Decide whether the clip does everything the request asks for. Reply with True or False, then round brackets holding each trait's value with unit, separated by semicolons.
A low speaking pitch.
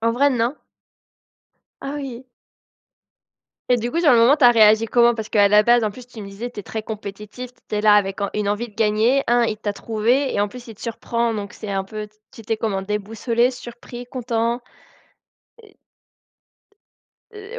False (230 Hz)